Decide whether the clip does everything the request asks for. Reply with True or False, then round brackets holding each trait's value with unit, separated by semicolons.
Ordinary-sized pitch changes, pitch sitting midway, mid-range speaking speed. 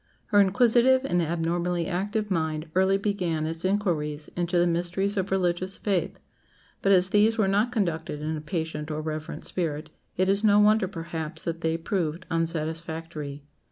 True (3.5 semitones; 175 Hz; 160 wpm)